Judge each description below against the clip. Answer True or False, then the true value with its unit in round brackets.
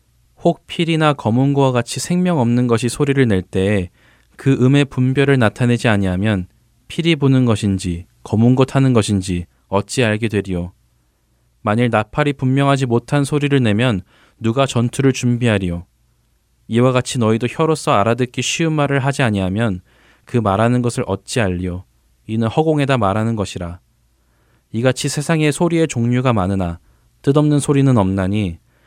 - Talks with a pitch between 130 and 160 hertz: False (120 Hz)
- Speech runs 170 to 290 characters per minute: False (320 characters per minute)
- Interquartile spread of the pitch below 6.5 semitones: True (5.6 semitones)